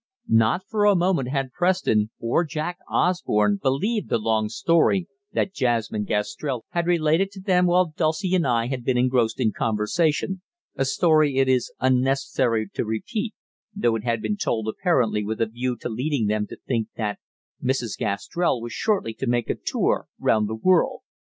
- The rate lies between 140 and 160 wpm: No, average, 175 wpm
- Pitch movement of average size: No, wide, 7.5 semitones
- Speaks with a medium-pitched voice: No, low, 130 Hz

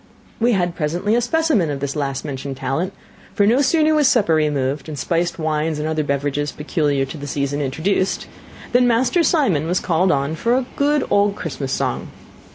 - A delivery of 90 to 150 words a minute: No, average, 185 wpm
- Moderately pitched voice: Yes, medium, 160 Hz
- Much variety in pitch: Yes, wide, 7.4 semitones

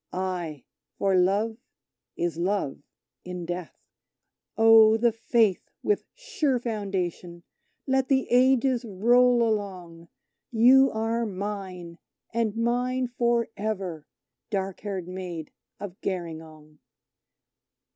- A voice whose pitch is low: No, high, 205 Hz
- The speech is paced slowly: Yes, slow, 100 wpm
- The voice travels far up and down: No, average, 4.7 semitones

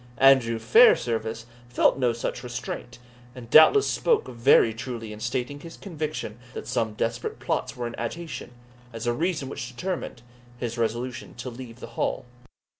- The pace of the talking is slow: No, average, 155 wpm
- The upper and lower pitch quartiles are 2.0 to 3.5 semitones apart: Yes, average, 2.8 semitones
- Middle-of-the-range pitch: No, low, 120 Hz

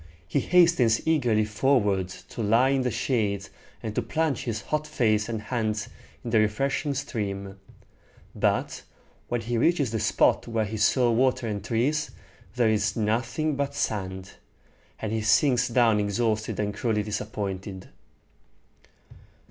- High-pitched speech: No, low, 115 Hz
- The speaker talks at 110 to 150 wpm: Yes, average, 140 wpm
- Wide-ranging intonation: No, average, 3.5 semitones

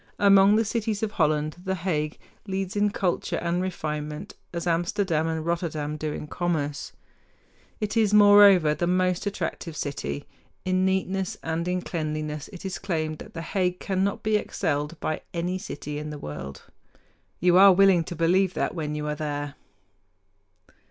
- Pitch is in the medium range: Yes, medium, 175 Hz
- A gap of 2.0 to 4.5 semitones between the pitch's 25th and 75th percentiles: Yes, average, 3.9 semitones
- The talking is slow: No, average, 160 wpm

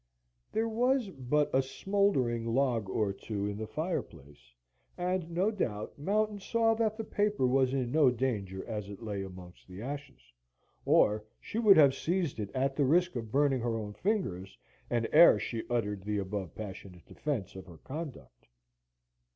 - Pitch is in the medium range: No, low, 125 Hz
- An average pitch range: No, wide, 8.7 semitones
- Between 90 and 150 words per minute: No, average, 165 wpm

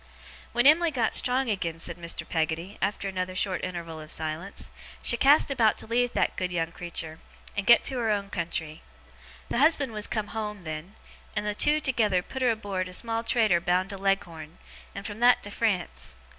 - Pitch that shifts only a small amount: No, average, 5.1 semitones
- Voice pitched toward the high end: Yes, high, 200 Hz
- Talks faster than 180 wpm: Yes, average, 195 wpm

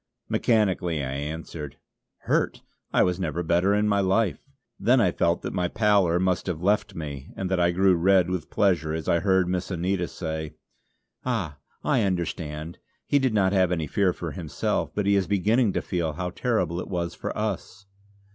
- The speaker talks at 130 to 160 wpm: No, average, 185 wpm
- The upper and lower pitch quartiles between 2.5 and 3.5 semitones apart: Yes, average, 3.0 semitones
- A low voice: Yes, very low, 90 Hz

